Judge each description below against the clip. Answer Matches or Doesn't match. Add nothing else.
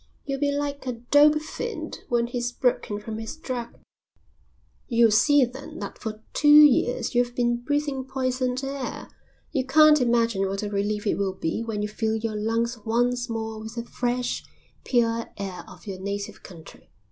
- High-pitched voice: Matches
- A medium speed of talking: Matches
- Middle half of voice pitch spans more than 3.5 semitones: Doesn't match